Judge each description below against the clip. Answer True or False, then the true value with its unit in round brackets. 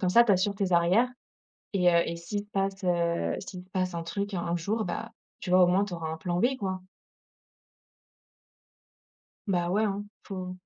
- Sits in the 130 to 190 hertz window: True (185 Hz)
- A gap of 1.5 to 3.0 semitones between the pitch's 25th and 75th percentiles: True (2.4 semitones)